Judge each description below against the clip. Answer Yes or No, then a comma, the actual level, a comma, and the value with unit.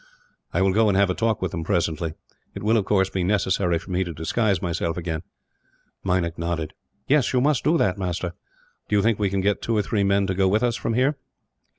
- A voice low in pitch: Yes, very low, 95 Hz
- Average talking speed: No, fast, 240 wpm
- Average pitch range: Yes, average, 3.5 semitones